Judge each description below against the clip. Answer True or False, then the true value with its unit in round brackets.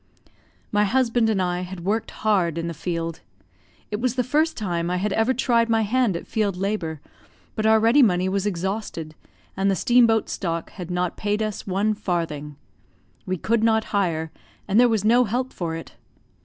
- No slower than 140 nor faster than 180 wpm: False (190 wpm)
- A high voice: True (205 Hz)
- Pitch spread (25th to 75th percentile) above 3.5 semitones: True (4.1 semitones)